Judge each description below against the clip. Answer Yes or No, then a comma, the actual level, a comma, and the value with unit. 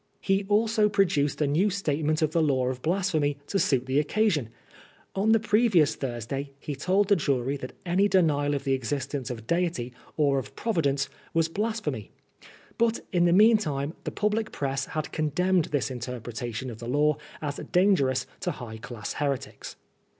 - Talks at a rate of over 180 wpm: No, average, 170 wpm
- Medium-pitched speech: Yes, medium, 150 Hz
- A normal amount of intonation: No, wide, 6.2 semitones